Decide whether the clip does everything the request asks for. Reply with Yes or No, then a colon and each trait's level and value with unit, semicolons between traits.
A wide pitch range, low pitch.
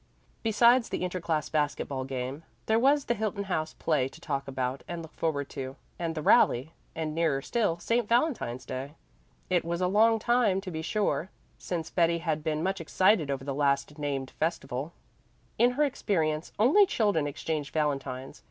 No: wide, 6.3 semitones; medium, 160 Hz